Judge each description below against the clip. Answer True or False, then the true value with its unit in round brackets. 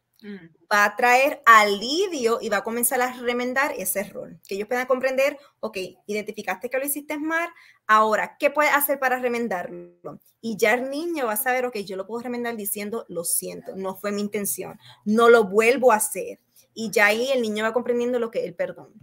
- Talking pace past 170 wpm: True (200 wpm)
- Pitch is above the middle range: True (230 Hz)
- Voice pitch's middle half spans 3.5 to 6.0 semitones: True (3.9 semitones)